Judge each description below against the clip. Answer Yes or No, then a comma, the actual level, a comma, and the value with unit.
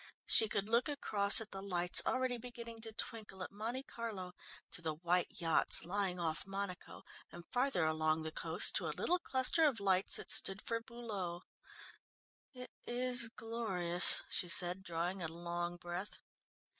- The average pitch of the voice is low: No, high, 195 Hz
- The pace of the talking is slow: No, average, 160 wpm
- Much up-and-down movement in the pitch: No, average, 5.0 semitones